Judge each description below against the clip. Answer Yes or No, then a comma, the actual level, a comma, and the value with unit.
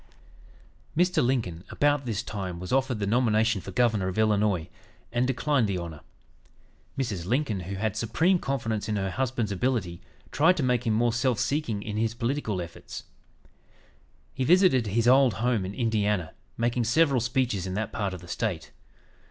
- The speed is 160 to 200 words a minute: Yes, average, 170 wpm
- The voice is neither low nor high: No, low, 115 Hz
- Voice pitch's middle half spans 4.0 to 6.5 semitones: Yes, average, 4.3 semitones